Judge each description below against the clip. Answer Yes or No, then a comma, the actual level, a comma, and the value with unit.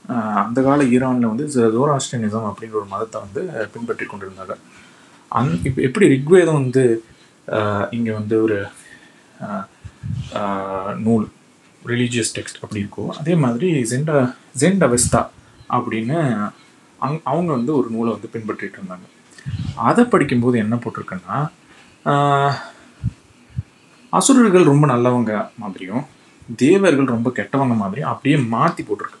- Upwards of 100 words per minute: Yes, average, 110 wpm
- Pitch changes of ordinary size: Yes, average, 4.2 semitones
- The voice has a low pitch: Yes, low, 120 Hz